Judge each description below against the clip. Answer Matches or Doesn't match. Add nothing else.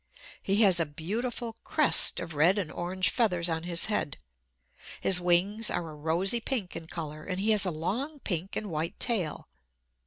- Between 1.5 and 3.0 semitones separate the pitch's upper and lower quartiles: Doesn't match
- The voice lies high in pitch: Doesn't match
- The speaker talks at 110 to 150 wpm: Doesn't match